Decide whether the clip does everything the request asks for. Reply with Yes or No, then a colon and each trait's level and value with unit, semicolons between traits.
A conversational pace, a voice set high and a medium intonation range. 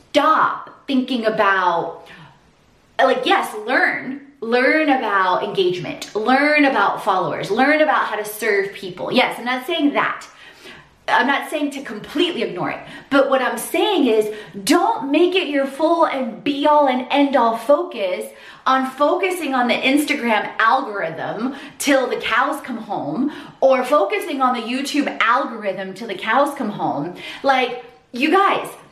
Yes: average, 150 wpm; very high, 270 Hz; average, 4.4 semitones